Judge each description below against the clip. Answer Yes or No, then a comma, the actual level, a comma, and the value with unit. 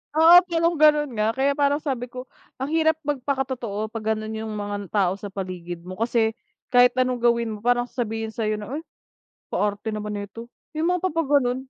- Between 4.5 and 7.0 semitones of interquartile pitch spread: Yes, average, 4.8 semitones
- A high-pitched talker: Yes, high, 240 Hz